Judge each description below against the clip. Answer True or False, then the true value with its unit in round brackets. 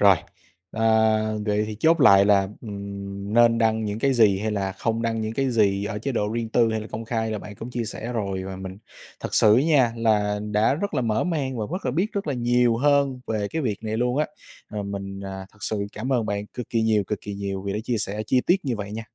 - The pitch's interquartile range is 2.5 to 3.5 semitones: True (3.1 semitones)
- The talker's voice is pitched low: True (110 Hz)